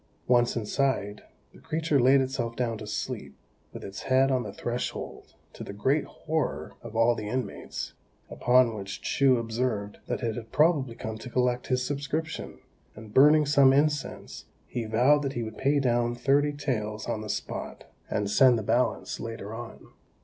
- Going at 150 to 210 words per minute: Yes, average, 170 wpm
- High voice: No, low, 125 Hz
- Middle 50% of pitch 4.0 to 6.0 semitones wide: No, average, 3.5 semitones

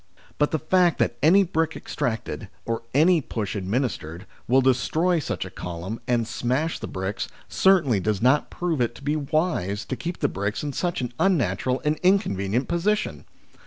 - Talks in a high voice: No, low, 135 Hz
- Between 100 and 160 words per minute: No, average, 170 wpm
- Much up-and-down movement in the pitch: Yes, wide, 6.8 semitones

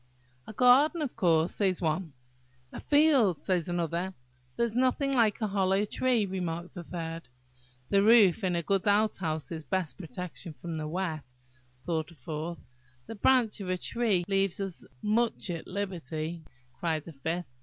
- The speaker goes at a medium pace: Yes, average, 160 wpm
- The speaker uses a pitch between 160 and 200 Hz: Yes, medium, 185 Hz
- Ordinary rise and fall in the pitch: Yes, average, 4.3 semitones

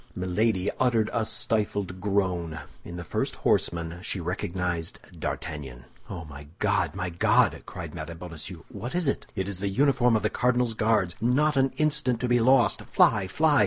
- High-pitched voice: No, low, 100 Hz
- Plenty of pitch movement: Yes, wide, 5.9 semitones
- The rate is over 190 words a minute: No, average, 170 wpm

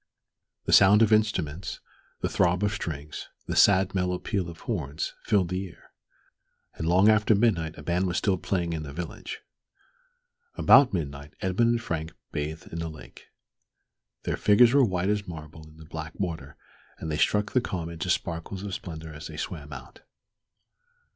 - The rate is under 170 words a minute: No, average, 175 wpm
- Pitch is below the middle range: Yes, very low, 85 Hz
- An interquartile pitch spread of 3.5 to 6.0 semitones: Yes, average, 4.0 semitones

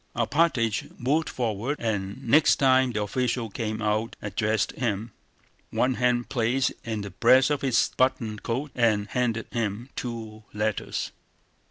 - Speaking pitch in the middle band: No, low, 115 Hz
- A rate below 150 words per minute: Yes, average, 140 wpm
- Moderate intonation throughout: Yes, average, 3.0 semitones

